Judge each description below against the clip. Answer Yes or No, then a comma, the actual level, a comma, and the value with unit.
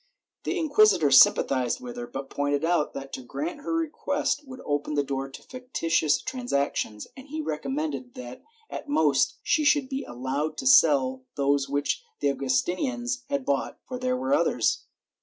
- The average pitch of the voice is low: No, medium, 150 Hz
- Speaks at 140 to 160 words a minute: No, average, 170 wpm